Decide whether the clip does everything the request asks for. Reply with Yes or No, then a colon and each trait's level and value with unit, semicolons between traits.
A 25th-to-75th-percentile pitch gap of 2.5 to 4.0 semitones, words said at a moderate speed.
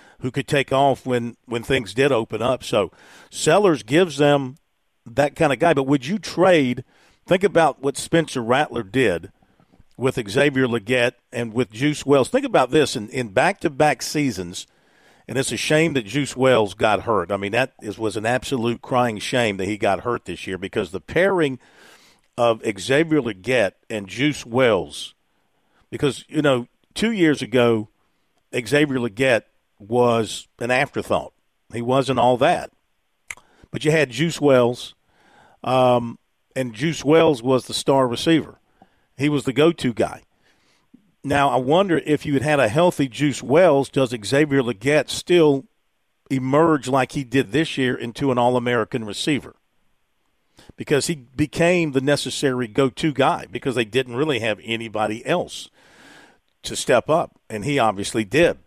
Yes: average, 3.5 semitones; average, 160 wpm